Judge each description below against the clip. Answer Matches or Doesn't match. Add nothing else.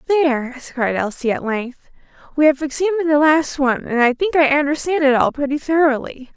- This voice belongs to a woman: Matches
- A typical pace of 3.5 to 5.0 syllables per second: Doesn't match